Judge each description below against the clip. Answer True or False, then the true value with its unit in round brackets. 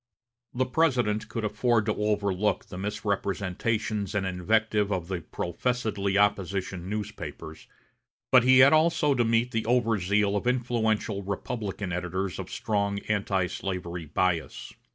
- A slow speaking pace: True (130 wpm)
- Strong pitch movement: False (3.3 semitones)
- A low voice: True (105 Hz)